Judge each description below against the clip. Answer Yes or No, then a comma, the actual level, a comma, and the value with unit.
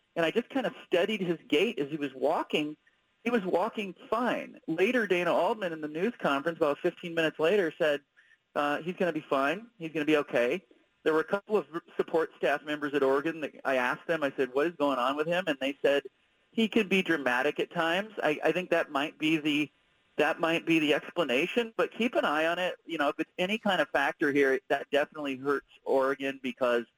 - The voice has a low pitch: No, medium, 165 Hz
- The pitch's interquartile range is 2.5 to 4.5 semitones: No, wide, 5.5 semitones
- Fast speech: Yes, fast, 230 wpm